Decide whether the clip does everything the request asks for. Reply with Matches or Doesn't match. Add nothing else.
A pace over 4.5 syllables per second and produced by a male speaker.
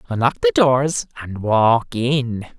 Doesn't match